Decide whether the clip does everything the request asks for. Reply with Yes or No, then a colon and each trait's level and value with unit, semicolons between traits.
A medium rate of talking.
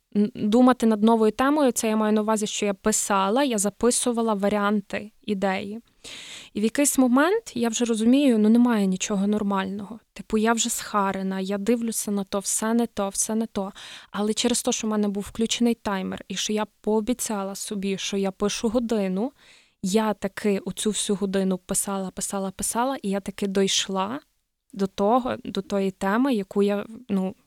No: fast, 175 wpm